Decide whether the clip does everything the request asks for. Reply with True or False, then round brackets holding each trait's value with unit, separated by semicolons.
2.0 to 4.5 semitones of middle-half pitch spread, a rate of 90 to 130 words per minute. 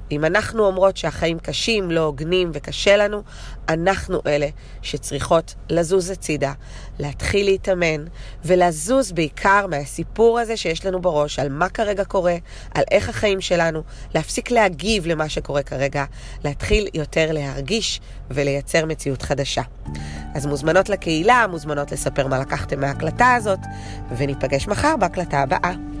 False (5.3 semitones; 125 wpm)